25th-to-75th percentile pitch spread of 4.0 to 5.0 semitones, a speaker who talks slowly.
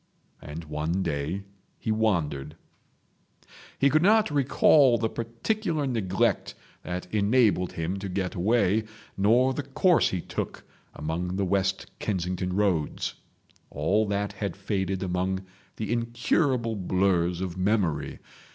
Yes: average, 4.4 semitones; slow, 125 wpm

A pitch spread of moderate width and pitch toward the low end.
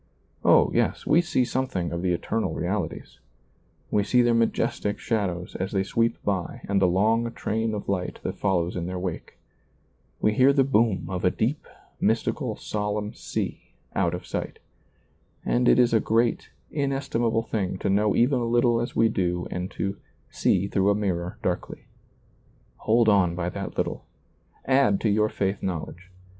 Yes: average, 4.0 semitones; low, 105 Hz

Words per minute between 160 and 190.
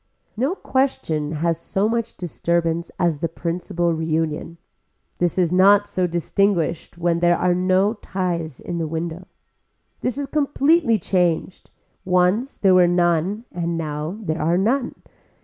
No: average, 140 wpm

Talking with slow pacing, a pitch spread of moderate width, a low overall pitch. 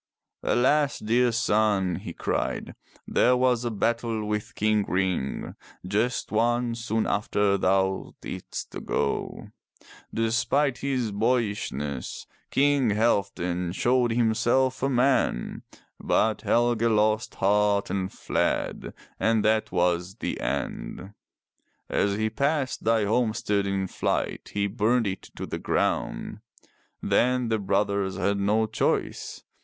Yes: slow, 115 wpm; average, 3.2 semitones; low, 110 Hz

